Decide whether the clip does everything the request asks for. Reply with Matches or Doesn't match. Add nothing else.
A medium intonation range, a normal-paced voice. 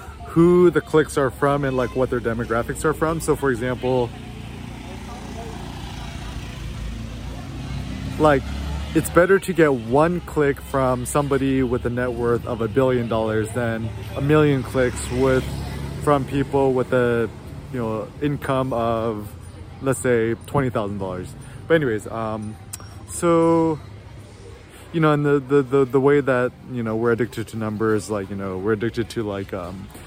Matches